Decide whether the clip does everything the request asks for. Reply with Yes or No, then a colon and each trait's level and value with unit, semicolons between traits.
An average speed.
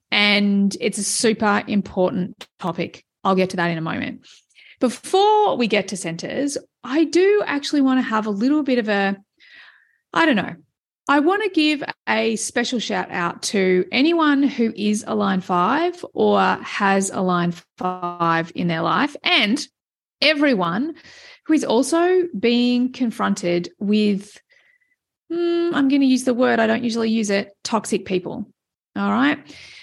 Yes: average, 160 wpm